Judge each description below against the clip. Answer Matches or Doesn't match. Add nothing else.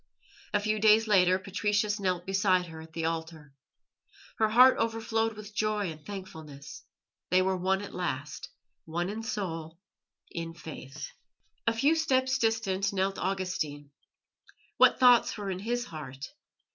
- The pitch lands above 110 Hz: Matches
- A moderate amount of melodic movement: Matches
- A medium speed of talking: Matches